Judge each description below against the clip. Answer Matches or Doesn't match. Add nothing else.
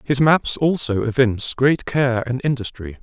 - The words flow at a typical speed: Matches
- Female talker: Doesn't match